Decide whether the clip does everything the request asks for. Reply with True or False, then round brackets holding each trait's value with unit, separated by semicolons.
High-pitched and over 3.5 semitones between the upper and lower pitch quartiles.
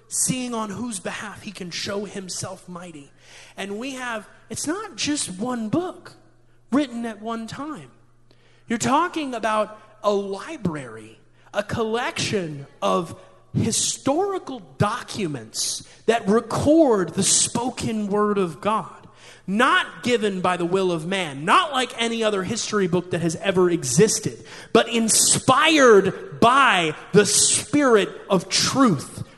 True (205 Hz; 5.3 semitones)